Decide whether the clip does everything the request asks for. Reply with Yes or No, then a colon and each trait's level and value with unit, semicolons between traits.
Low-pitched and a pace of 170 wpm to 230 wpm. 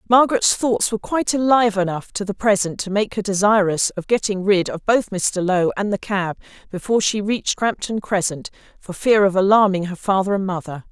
No: high, 200 Hz; average, 200 wpm